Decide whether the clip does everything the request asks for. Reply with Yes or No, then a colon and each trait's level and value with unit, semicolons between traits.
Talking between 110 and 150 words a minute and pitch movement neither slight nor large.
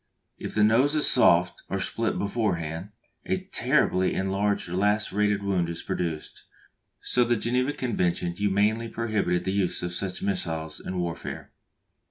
Yes: average, 145 wpm; average, 4.4 semitones